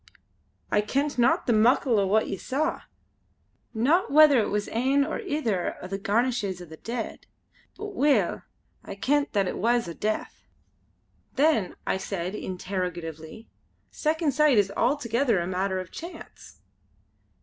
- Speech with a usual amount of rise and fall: No, wide, 6.6 semitones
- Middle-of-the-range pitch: No, high, 225 Hz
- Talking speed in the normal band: Yes, average, 150 wpm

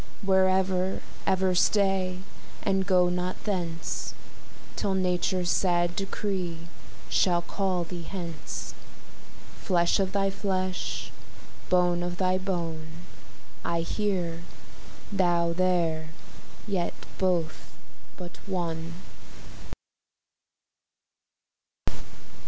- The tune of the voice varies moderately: No, narrow, 1.7 semitones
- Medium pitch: Yes, medium, 180 Hz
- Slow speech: Yes, slow, 85 wpm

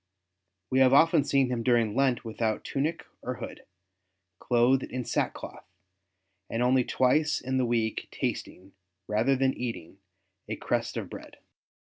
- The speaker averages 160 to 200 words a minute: No, average, 140 wpm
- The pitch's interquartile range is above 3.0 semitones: No, narrow, 2.5 semitones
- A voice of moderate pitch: No, low, 125 Hz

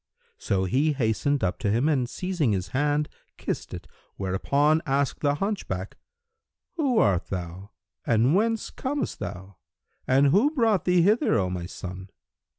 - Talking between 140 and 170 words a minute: Yes, average, 150 wpm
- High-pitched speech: No, low, 135 Hz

